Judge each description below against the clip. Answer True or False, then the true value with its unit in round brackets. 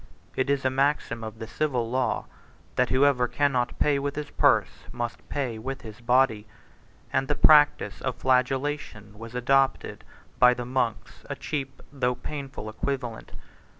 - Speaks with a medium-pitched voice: False (130 Hz)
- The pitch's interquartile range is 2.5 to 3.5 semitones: True (2.8 semitones)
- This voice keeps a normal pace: True (150 wpm)